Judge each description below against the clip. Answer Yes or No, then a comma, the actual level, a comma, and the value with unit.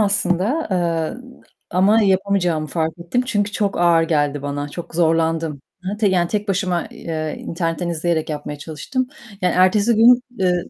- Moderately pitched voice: Yes, medium, 175 Hz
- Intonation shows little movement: No, average, 3.8 semitones